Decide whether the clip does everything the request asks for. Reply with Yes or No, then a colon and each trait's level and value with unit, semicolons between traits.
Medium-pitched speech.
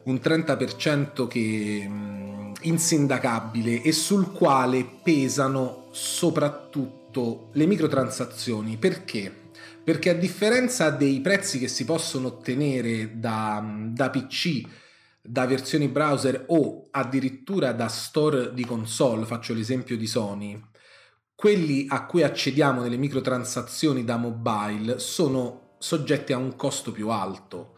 No: low, 130 Hz